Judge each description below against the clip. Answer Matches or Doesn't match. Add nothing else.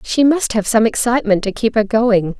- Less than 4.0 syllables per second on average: Doesn't match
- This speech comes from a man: Doesn't match